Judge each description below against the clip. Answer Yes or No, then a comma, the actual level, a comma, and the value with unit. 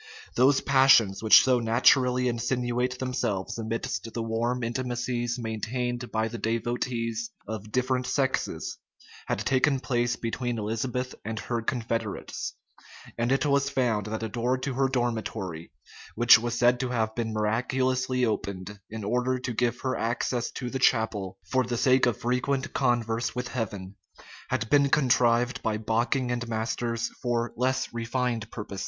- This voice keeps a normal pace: Yes, average, 150 wpm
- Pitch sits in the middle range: No, low, 120 Hz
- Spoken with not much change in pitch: Yes, narrow, 2.1 semitones